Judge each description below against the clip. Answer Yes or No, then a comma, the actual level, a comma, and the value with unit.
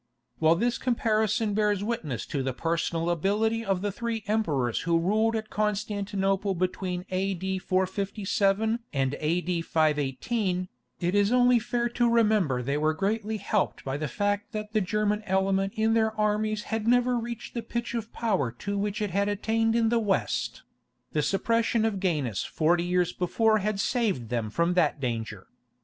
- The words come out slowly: No, average, 165 wpm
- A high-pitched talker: Yes, high, 200 Hz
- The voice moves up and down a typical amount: Yes, average, 4.3 semitones